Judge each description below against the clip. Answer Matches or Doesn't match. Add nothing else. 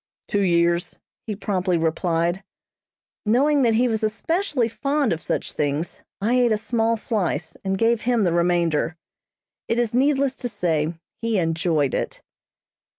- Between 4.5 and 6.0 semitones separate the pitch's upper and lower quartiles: Matches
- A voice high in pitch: Matches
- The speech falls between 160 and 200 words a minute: Doesn't match